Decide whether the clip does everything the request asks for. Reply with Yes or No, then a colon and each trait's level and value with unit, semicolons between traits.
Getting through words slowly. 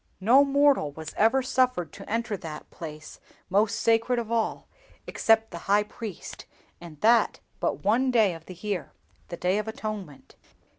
No: average, 160 wpm